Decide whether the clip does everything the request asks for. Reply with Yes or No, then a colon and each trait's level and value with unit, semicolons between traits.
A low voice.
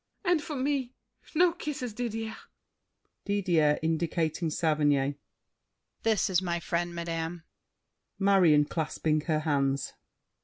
No: medium, 170 Hz